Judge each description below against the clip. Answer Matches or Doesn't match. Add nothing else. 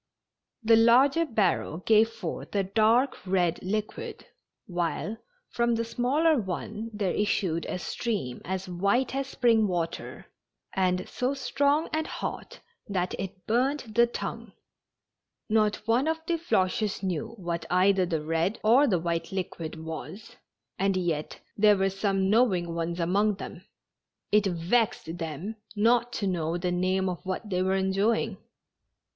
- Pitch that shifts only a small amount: Doesn't match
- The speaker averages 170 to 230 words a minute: Doesn't match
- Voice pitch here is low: Doesn't match